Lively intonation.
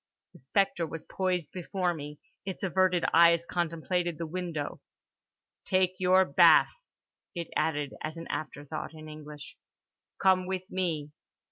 No: average, 3.0 semitones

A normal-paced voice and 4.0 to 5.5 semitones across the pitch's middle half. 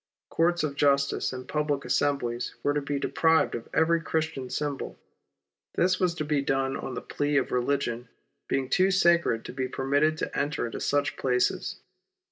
No: average, 170 wpm; average, 3.1 semitones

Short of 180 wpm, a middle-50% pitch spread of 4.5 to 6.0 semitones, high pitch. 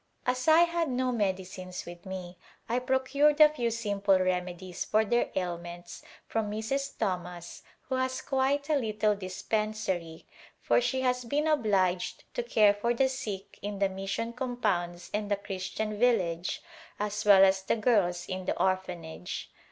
Yes: average, 160 wpm; average, 5.2 semitones; high, 210 Hz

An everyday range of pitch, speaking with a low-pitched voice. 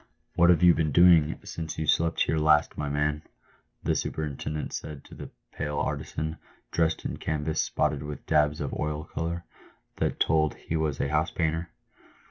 No: narrow, 1.5 semitones; very low, 75 Hz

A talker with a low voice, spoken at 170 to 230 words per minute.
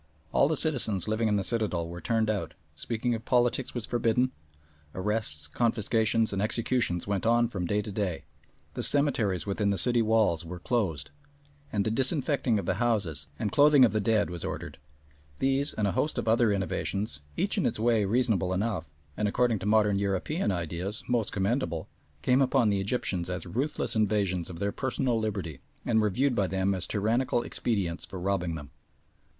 Yes: low, 105 Hz; average, 180 wpm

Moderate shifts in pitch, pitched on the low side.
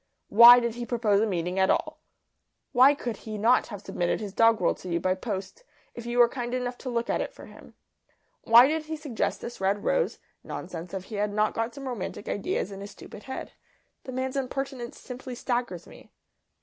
No: average, 3.8 semitones; high, 235 Hz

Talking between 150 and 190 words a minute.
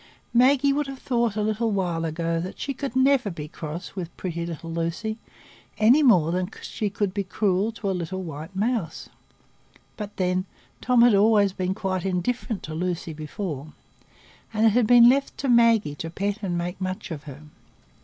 Yes: average, 185 wpm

